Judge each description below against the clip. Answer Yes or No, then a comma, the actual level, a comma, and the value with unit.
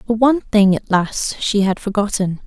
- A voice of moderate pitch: No, high, 210 Hz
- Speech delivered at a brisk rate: No, average, 145 wpm